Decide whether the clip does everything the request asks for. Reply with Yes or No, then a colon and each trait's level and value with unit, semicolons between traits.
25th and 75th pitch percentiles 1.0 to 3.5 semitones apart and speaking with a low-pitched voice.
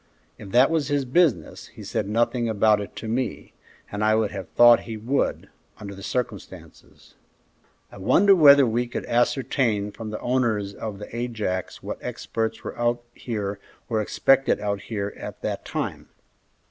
Yes: average, 3.1 semitones; low, 115 Hz